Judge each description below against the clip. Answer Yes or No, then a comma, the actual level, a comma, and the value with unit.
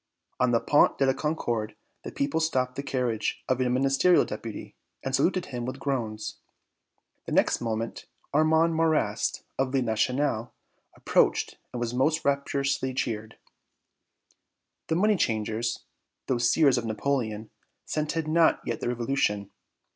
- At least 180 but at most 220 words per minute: No, average, 140 wpm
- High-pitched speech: No, low, 130 Hz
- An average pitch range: Yes, average, 4.0 semitones